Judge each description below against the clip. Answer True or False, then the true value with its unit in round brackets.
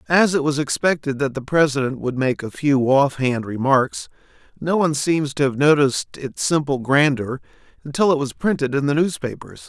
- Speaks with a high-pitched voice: False (140 Hz)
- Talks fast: False (180 wpm)